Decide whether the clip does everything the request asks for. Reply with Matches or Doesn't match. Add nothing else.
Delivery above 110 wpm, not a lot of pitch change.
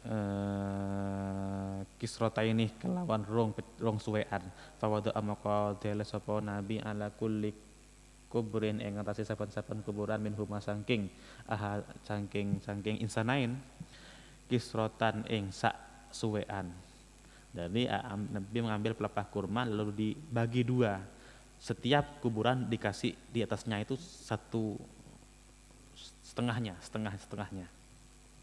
Doesn't match